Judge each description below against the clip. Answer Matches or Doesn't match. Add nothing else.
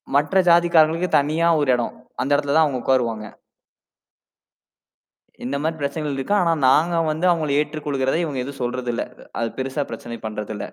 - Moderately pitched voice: Matches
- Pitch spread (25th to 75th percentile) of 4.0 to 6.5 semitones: Doesn't match